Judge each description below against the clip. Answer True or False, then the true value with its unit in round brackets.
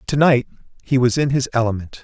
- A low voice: True (125 Hz)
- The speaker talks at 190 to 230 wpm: True (205 wpm)